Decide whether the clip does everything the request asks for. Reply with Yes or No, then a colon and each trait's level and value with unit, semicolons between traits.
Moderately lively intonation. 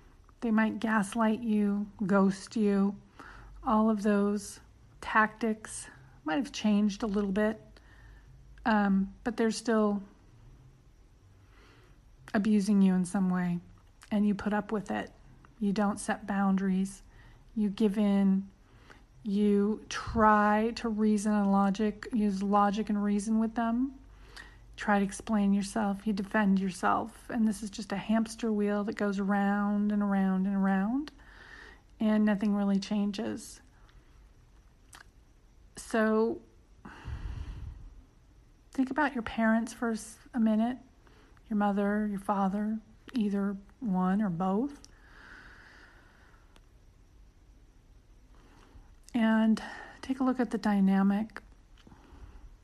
No: narrow, 2.0 semitones